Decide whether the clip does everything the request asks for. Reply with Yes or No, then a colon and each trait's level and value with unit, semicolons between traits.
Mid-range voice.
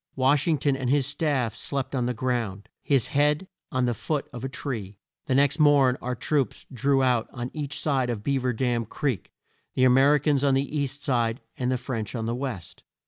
No: low, 130 Hz